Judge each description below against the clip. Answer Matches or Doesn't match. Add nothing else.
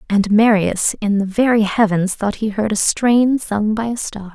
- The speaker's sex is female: Matches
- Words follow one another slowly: Doesn't match